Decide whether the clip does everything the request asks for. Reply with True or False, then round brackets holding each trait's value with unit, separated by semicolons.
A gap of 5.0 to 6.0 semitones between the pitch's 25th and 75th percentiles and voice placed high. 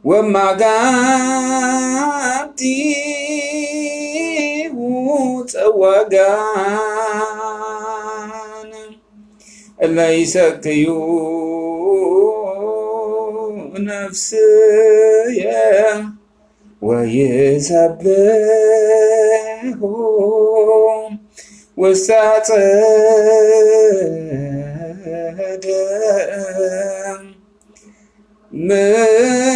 False (2.5 semitones; 215 Hz)